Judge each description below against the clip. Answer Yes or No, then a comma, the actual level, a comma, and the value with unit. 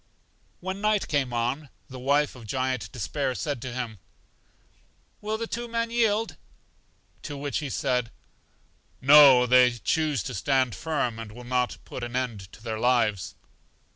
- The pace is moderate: Yes, average, 160 wpm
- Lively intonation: No, average, 3.9 semitones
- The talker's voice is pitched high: No, low, 130 Hz